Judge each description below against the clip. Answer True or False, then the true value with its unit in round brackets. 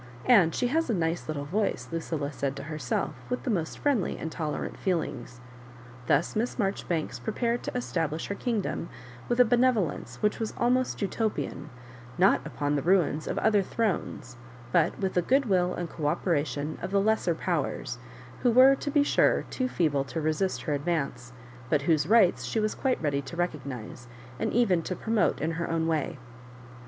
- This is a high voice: False (175 Hz)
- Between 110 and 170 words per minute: False (180 wpm)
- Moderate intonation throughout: False (6.4 semitones)